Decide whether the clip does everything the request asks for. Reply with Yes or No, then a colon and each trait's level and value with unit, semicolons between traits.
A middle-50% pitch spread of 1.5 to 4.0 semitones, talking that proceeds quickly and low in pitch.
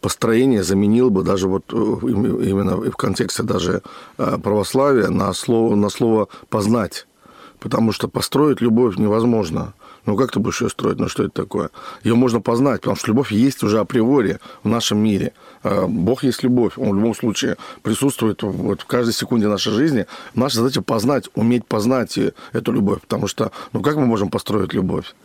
Yes: average, 2.8 semitones; fast, 170 wpm; low, 115 Hz